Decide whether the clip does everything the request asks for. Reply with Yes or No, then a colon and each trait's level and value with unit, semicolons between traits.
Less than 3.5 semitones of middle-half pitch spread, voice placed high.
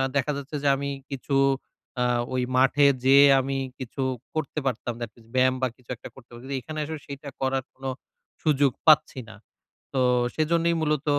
No: narrow, 2.5 semitones; low, 135 Hz